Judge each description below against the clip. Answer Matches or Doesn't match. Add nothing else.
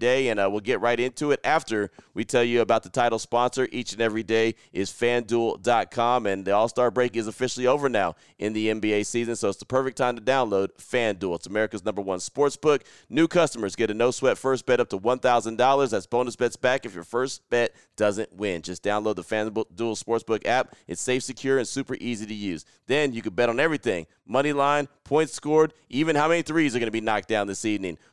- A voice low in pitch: Matches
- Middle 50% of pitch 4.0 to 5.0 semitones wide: Doesn't match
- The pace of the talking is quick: Matches